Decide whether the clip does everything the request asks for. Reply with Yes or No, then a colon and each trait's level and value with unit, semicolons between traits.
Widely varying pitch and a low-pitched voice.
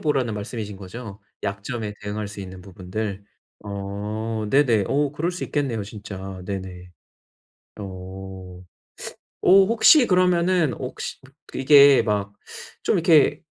Yes: wide, 6.1 semitones; low, 105 Hz